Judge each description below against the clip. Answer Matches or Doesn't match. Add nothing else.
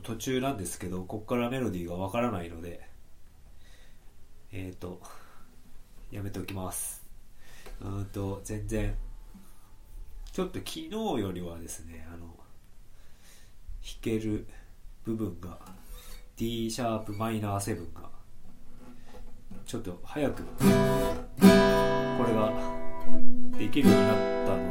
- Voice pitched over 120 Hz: Doesn't match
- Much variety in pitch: Doesn't match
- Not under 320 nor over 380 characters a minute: Doesn't match